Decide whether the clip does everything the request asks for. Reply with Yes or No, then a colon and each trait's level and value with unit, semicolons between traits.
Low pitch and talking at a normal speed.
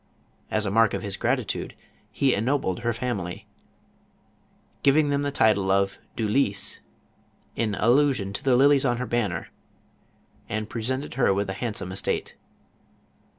Yes: low, 115 Hz; average, 150 wpm